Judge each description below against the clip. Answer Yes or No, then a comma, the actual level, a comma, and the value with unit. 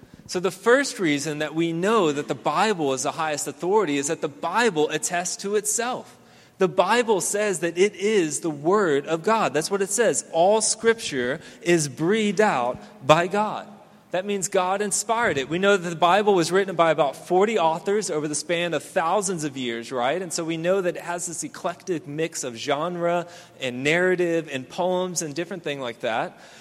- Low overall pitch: No, medium, 175 Hz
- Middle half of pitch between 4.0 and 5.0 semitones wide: Yes, average, 4.4 semitones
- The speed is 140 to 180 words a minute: No, average, 195 wpm